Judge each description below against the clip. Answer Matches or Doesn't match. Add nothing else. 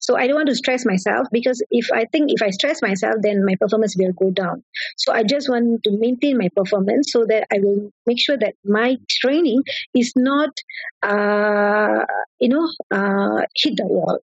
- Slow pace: Doesn't match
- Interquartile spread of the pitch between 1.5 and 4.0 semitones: Doesn't match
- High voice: Matches